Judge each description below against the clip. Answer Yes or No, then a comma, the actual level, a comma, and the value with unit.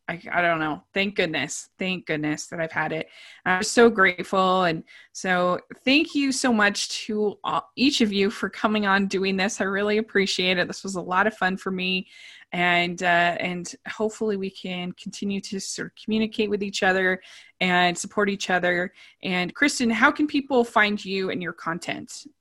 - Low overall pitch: No, high, 195 Hz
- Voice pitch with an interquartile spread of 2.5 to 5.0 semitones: Yes, average, 3.2 semitones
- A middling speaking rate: Yes, average, 190 wpm